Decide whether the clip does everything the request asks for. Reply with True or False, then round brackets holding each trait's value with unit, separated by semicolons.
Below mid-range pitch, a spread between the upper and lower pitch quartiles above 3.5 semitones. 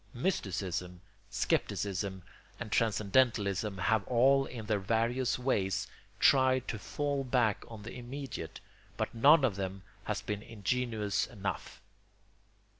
True (110 Hz; 4.3 semitones)